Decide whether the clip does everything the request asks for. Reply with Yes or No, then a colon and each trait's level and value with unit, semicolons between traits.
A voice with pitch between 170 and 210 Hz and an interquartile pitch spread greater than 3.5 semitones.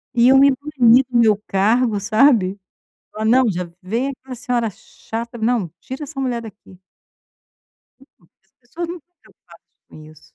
No: high, 235 Hz; average, 4.0 semitones